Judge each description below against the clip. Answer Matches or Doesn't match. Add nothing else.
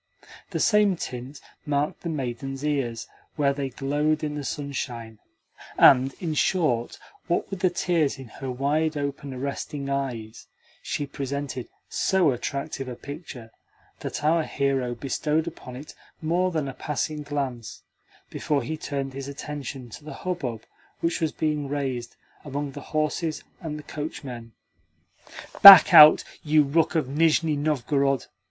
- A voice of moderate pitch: Matches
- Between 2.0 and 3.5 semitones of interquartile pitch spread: Matches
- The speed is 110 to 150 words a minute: Matches